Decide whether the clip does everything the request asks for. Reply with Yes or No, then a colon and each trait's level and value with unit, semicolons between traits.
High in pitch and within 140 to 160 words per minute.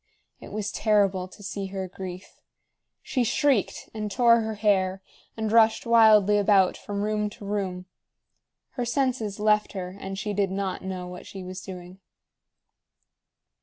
Yes: high, 205 Hz; average, 150 wpm